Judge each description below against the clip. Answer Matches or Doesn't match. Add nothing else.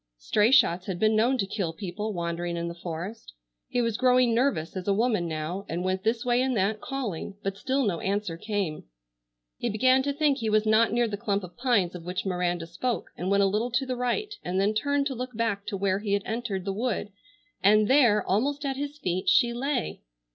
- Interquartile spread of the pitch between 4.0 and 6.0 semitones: Matches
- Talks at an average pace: Doesn't match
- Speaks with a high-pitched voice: Matches